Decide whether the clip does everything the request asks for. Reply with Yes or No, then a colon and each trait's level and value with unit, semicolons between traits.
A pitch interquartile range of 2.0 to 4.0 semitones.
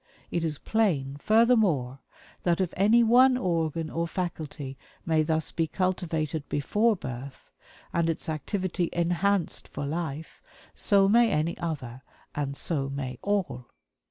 No: average, 5.1 semitones